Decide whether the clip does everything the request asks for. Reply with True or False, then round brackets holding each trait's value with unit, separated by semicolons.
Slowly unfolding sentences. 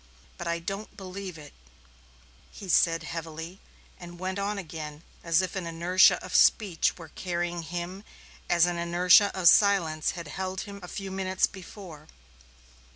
False (155 wpm)